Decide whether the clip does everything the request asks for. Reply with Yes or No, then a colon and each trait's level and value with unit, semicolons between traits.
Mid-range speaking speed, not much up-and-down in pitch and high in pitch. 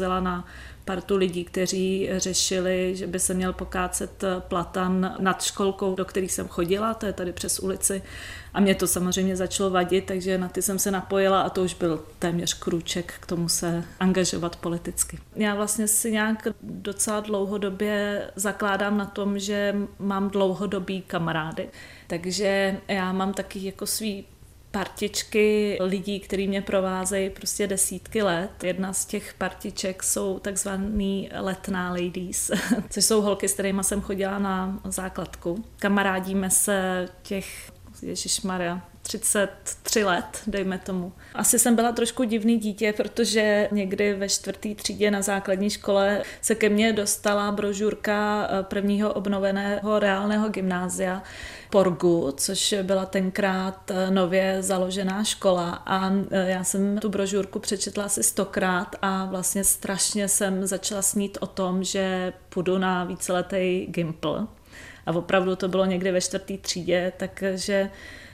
Yes: average, 140 wpm; narrow, 1.5 semitones; high, 195 Hz